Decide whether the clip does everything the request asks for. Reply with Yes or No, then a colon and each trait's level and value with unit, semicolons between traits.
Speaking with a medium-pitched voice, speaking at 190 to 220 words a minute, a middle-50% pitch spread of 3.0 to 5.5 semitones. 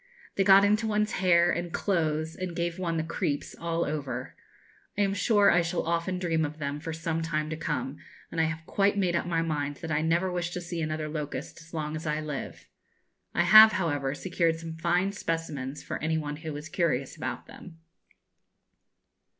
No: medium, 165 Hz; average, 200 wpm; narrow, 2.4 semitones